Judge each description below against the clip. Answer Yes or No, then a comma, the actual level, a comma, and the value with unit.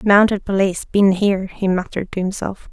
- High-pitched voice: Yes, high, 195 Hz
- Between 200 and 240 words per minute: No, average, 175 wpm